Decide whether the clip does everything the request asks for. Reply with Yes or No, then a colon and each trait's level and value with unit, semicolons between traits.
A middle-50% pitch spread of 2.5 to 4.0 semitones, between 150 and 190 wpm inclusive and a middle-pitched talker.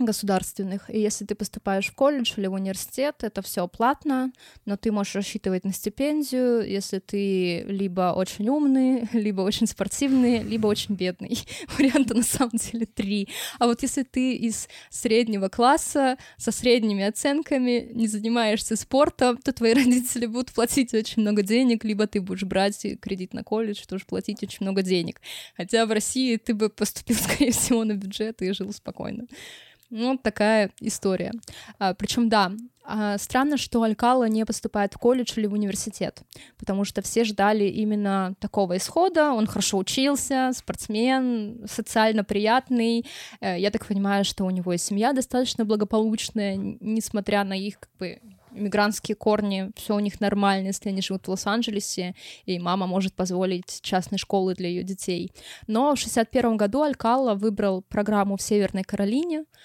No: average, 3.3 semitones; average, 155 wpm; high, 215 Hz